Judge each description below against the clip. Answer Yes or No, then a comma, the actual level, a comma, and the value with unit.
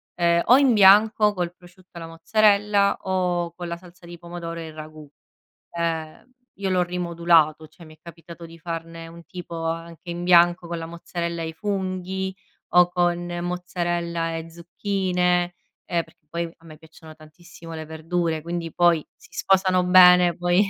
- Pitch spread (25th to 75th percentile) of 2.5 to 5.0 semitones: No, narrow, 1.4 semitones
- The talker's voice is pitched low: No, medium, 175 Hz